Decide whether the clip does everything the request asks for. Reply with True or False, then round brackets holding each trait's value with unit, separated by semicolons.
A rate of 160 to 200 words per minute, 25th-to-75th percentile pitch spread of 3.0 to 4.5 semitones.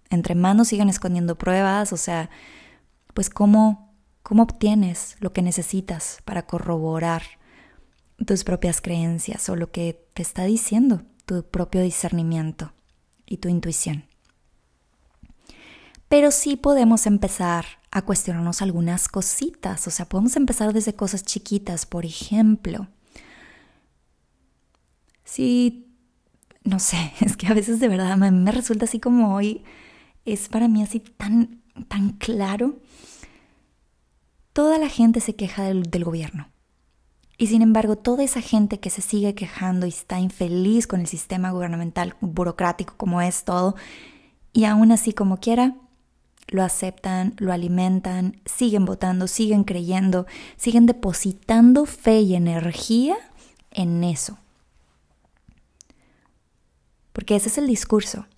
False (130 wpm; 4.0 semitones)